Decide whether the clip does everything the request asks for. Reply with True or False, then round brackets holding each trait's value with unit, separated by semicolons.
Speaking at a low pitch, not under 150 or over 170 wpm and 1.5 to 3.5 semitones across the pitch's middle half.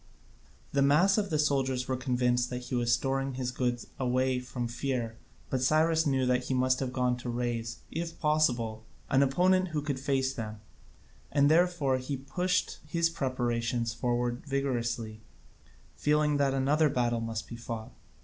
True (130 Hz; 160 wpm; 2.9 semitones)